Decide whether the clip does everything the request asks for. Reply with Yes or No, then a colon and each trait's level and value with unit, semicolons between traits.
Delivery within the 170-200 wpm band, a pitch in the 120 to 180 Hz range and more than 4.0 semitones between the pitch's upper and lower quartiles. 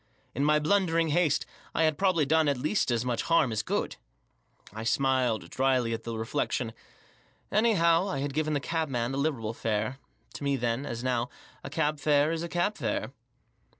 Yes: average, 185 wpm; medium, 140 Hz; average, 4.9 semitones